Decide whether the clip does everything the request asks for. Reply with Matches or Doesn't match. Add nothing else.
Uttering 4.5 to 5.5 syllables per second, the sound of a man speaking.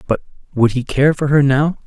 Matches